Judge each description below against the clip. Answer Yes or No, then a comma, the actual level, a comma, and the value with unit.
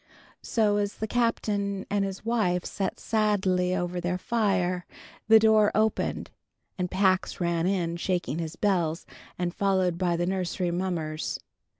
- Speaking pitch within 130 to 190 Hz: Yes, medium, 185 Hz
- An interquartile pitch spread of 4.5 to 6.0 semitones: No, narrow, 2.6 semitones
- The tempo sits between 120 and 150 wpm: Yes, average, 140 wpm